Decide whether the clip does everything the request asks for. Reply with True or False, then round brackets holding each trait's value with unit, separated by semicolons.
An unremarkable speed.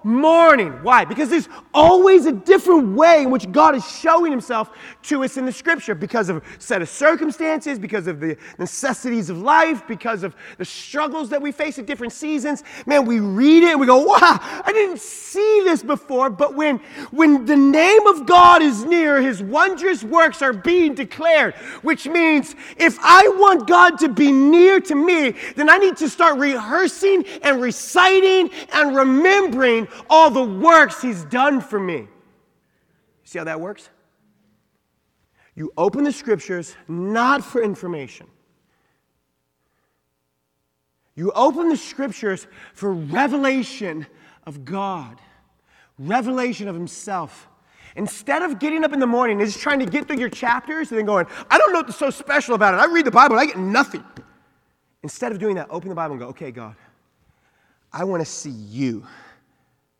True (170 wpm)